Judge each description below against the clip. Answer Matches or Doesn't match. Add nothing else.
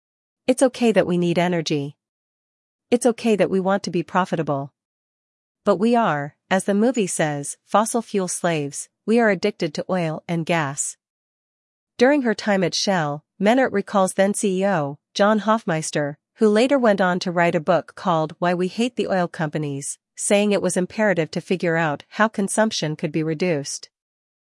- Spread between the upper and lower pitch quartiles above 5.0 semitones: Doesn't match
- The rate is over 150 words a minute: Matches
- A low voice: Doesn't match